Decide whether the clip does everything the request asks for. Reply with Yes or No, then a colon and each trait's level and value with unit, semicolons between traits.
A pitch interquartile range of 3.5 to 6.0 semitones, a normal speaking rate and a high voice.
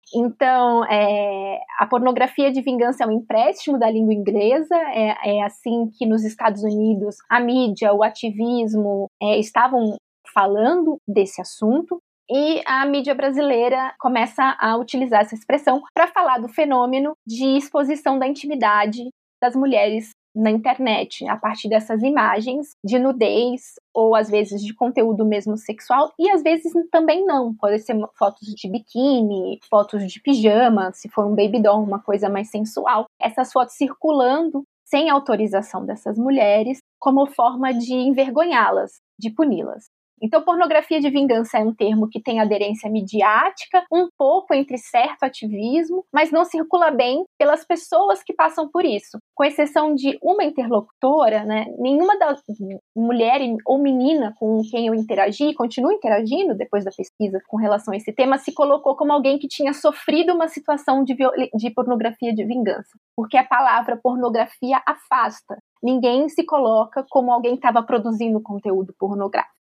Yes: average, 4.7 semitones; average, 150 wpm; high, 245 Hz